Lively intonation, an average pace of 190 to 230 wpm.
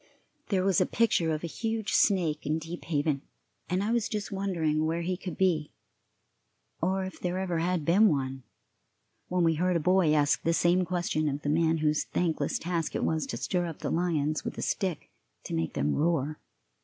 No: average, 3.1 semitones; average, 200 wpm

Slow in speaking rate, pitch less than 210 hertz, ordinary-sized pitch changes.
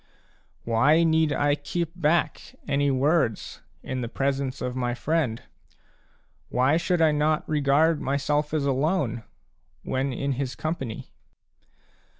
Yes: slow, 125 wpm; medium, 140 Hz; average, 3.2 semitones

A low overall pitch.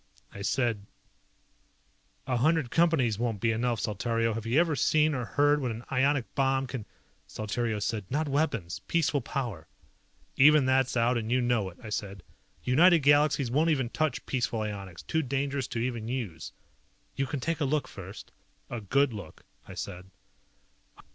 Yes: low, 125 Hz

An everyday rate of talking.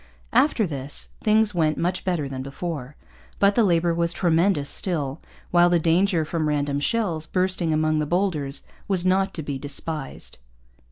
Yes: average, 160 wpm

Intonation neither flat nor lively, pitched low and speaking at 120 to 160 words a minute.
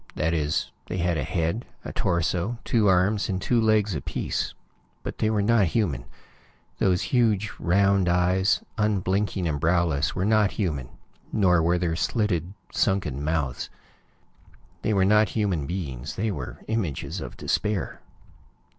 Yes: average, 4.1 semitones; very low, 95 Hz; average, 145 wpm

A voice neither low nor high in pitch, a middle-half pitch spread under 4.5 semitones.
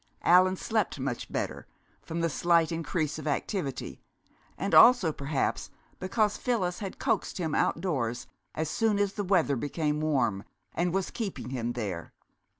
No: medium, 165 Hz; wide, 5.6 semitones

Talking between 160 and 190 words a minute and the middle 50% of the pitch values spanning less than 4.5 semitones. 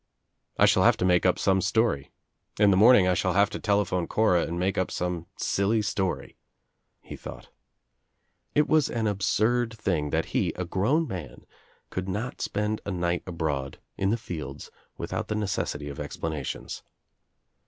Yes: average, 170 wpm; average, 3.6 semitones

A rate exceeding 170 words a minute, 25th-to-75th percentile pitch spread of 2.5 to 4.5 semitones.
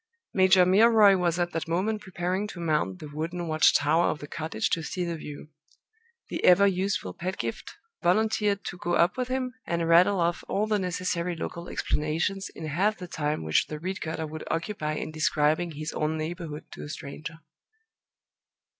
Yes: average, 180 wpm; average, 3.3 semitones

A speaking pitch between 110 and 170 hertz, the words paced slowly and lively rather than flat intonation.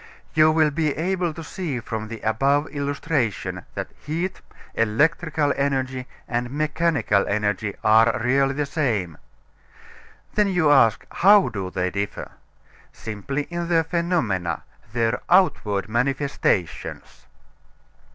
Yes: medium, 140 Hz; slow, 115 wpm; wide, 6.4 semitones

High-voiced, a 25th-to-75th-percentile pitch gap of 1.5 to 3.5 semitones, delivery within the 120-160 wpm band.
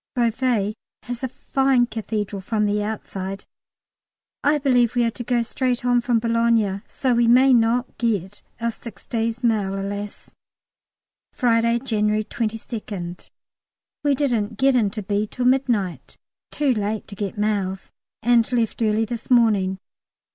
Yes: high, 230 Hz; average, 2.8 semitones; average, 145 wpm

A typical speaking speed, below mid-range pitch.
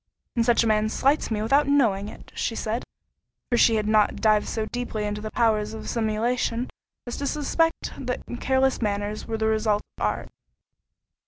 No: average, 180 wpm; high, 225 Hz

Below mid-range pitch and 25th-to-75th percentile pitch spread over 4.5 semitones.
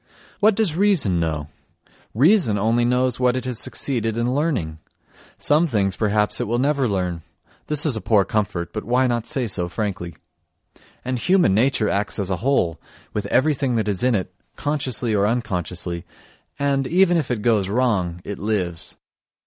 Yes: low, 115 Hz; wide, 5.5 semitones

